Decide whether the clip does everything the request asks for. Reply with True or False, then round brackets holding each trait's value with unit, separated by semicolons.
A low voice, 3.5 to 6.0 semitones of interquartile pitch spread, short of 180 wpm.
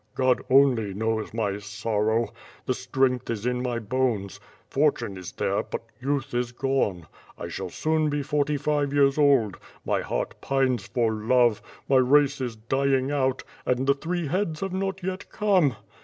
True (130 Hz; 3.9 semitones; 165 wpm)